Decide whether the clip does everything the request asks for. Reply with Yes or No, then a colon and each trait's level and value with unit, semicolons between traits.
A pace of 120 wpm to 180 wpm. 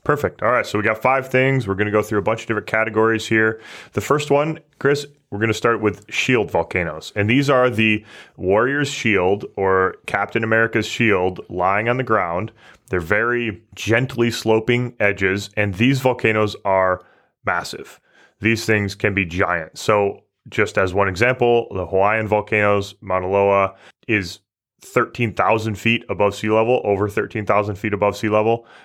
Yes: average, 170 wpm